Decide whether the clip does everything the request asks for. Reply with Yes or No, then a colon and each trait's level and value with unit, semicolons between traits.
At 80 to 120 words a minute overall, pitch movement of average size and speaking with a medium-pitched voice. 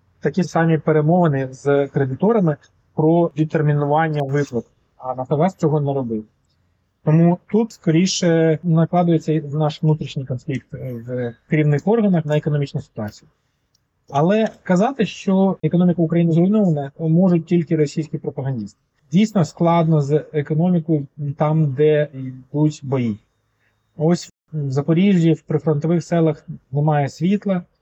Yes: average, 110 wpm; average, 3.2 semitones; medium, 155 Hz